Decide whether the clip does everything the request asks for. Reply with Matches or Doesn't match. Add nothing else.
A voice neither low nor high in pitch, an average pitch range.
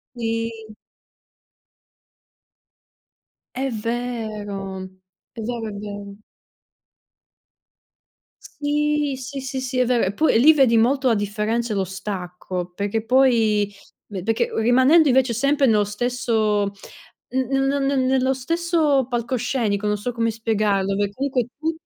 Doesn't match